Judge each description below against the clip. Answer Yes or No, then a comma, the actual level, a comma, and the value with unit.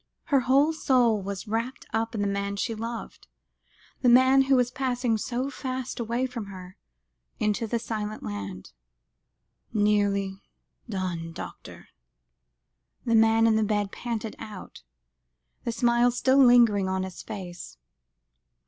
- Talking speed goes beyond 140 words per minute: No, slow, 135 wpm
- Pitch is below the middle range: No, high, 225 Hz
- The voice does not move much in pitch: No, average, 3.6 semitones